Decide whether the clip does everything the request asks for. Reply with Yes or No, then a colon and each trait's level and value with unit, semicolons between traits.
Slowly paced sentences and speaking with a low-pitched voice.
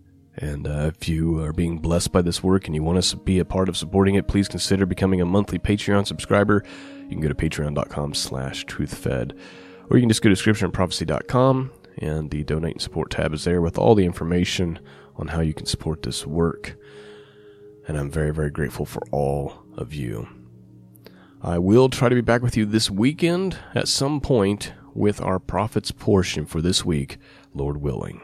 No: average, 195 wpm; very low, 90 Hz